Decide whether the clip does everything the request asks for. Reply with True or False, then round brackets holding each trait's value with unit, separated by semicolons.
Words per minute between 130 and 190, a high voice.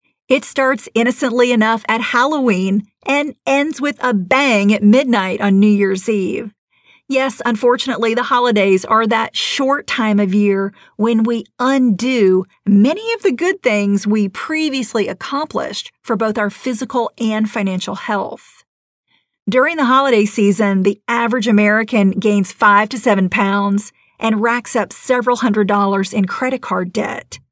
True (145 wpm; 225 Hz)